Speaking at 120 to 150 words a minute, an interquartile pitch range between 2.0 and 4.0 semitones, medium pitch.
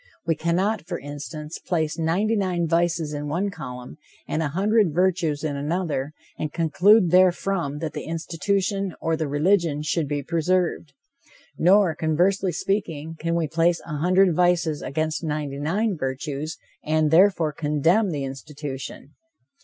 Yes: average, 145 wpm; average, 3.4 semitones; medium, 165 Hz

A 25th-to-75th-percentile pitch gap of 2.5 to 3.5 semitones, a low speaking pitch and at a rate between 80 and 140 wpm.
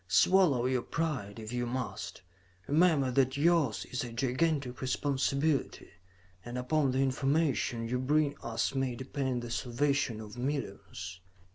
Yes: average, 3.0 semitones; low, 130 Hz; slow, 135 wpm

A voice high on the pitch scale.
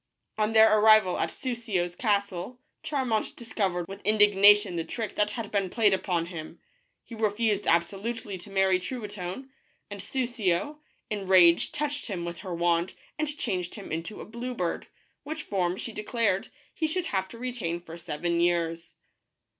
Yes: high, 200 Hz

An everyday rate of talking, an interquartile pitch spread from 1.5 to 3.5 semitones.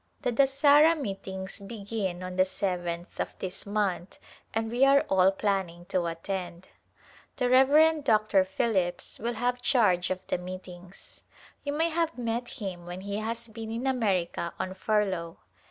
No: average, 155 wpm; average, 4.8 semitones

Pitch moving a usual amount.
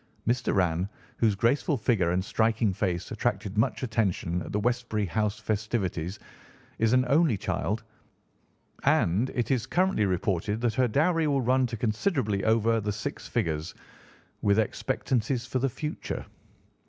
Yes: average, 3.8 semitones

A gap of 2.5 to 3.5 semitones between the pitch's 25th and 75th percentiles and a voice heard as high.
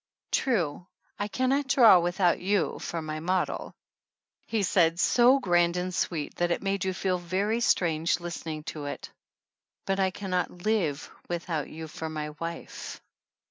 No: average, 3.2 semitones; medium, 175 Hz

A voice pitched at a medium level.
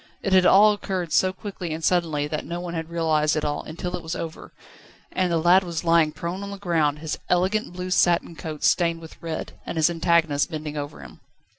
Yes: medium, 170 Hz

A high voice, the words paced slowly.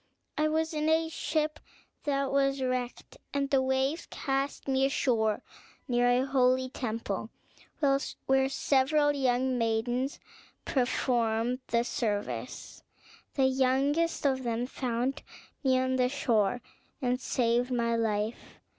Yes: very high, 260 Hz; slow, 120 wpm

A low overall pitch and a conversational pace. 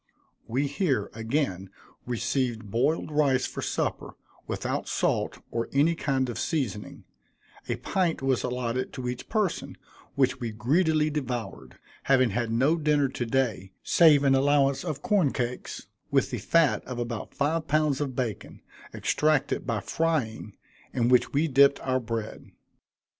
Yes: low, 130 Hz; average, 145 wpm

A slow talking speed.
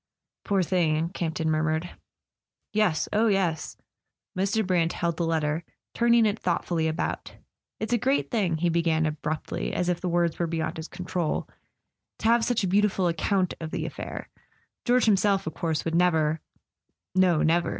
No: average, 165 wpm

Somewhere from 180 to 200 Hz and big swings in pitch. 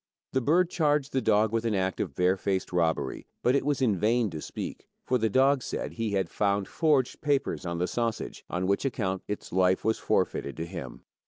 No: low, 105 Hz; wide, 5.9 semitones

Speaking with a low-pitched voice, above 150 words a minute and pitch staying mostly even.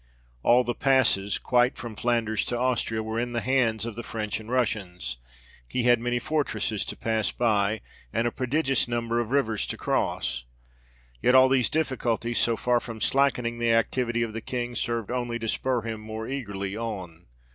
Yes: low, 115 Hz; average, 180 wpm; narrow, 2.0 semitones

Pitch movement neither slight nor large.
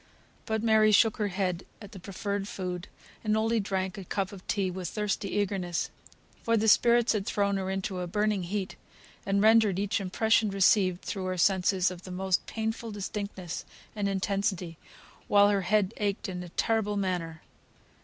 No: narrow, 2.2 semitones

